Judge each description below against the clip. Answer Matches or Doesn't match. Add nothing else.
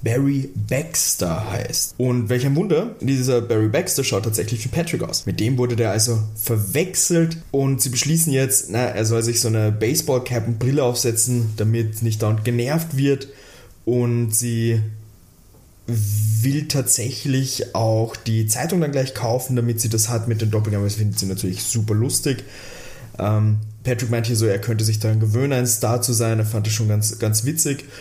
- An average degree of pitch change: Matches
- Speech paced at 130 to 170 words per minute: Doesn't match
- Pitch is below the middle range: Matches